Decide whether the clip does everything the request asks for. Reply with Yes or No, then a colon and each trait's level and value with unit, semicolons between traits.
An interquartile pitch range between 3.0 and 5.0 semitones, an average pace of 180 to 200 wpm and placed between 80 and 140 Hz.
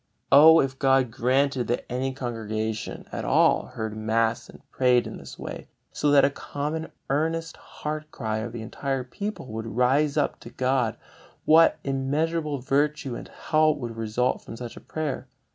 No: average, 4.1 semitones; average, 165 wpm; low, 135 Hz